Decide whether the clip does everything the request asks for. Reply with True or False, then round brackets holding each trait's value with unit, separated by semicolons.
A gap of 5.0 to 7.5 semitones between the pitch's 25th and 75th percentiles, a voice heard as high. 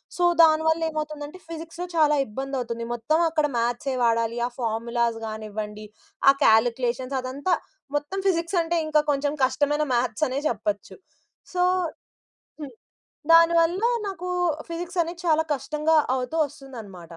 True (5.6 semitones; 290 Hz)